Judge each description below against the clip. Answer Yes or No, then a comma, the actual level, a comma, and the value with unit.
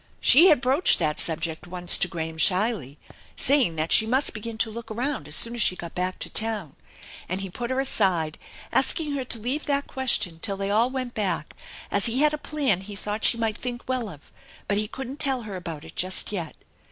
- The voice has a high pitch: Yes, high, 215 Hz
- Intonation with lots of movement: Yes, wide, 6.2 semitones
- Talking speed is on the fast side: Yes, fast, 220 wpm